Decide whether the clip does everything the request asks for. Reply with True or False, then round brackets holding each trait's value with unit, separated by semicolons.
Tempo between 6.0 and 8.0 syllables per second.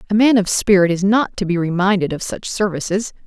False (5.8 syllables/s)